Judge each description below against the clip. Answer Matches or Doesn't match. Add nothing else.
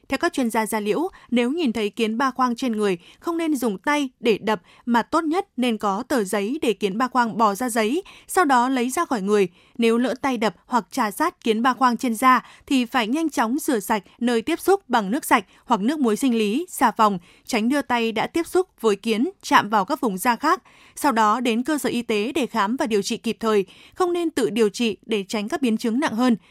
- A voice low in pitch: Doesn't match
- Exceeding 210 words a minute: Matches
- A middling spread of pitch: Matches